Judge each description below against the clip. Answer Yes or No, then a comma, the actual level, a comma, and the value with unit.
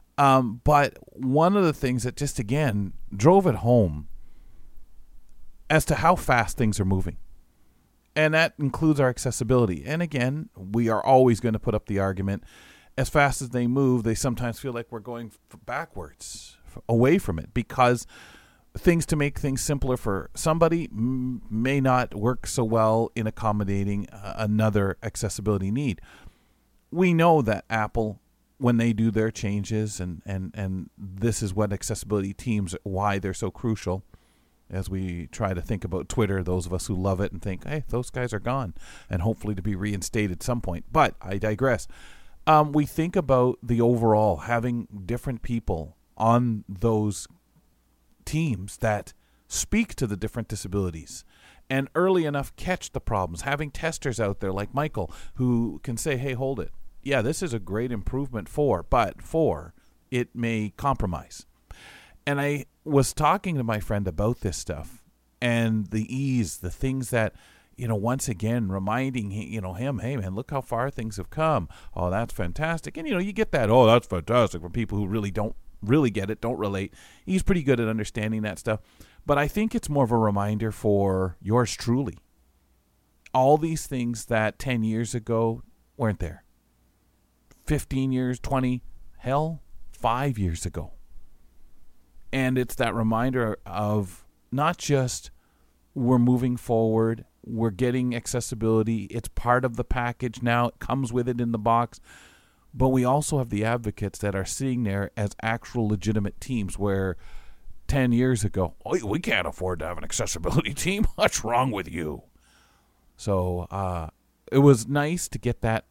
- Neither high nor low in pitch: No, low, 115 Hz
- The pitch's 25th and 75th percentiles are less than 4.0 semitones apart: No, average, 4.7 semitones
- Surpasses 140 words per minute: Yes, average, 165 wpm